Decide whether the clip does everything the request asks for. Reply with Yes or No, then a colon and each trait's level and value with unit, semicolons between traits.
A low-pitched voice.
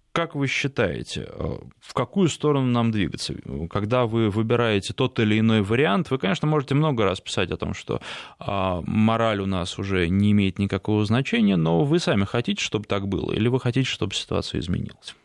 Yes: low, 110 Hz